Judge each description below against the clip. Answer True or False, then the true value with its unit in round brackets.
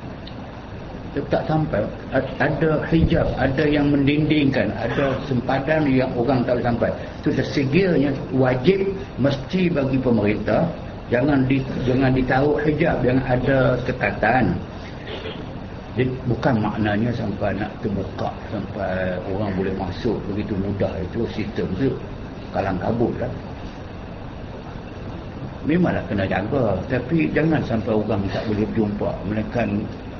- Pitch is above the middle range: False (120 Hz)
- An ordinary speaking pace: True (120 wpm)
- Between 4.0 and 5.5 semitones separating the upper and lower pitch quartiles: True (4.8 semitones)